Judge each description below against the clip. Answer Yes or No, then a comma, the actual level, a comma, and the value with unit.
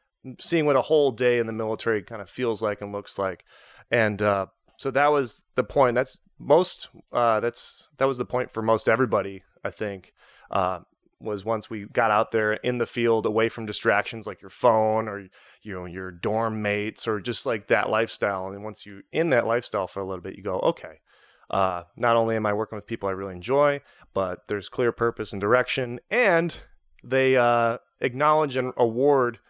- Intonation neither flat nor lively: Yes, average, 3.5 semitones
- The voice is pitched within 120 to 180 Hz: No, low, 110 Hz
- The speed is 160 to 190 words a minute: No, average, 200 wpm